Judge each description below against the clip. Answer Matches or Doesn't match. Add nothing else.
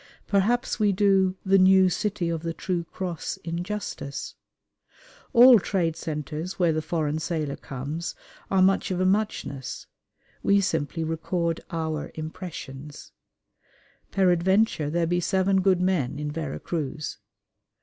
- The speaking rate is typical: Doesn't match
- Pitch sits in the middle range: Matches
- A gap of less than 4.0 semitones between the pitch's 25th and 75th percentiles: Matches